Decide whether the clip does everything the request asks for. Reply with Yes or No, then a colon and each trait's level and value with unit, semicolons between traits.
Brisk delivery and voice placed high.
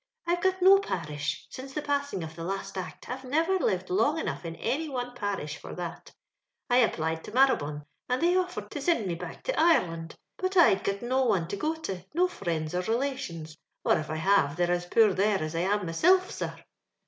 Yes: fast, 210 wpm; high, 205 Hz